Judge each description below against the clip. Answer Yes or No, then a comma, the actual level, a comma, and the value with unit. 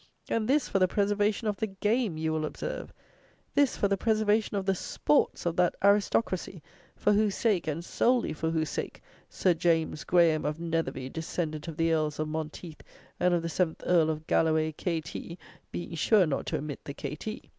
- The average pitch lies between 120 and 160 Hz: No, medium, 170 Hz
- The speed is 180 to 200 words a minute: Yes, average, 190 wpm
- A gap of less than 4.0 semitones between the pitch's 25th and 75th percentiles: No, average, 4.4 semitones